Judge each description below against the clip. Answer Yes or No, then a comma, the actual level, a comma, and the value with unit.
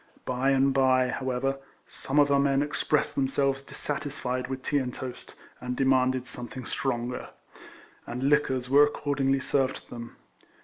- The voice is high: No, low, 135 Hz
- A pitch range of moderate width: No, narrow, 1.5 semitones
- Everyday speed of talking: Yes, average, 145 wpm